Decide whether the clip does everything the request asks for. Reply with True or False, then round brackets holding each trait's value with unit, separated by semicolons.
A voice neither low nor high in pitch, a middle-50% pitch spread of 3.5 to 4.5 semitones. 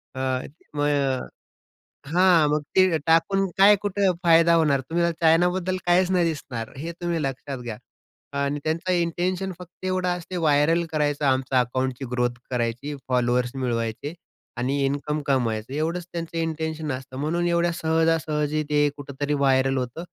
True (150 Hz; 4.2 semitones)